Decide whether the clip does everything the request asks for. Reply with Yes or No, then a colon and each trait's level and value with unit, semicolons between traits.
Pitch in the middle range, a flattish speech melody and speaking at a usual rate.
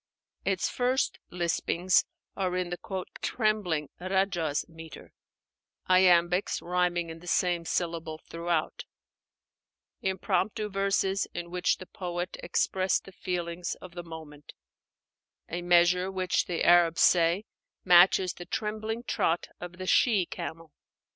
No: medium, 180 Hz; narrow, 1.9 semitones; slow, 120 wpm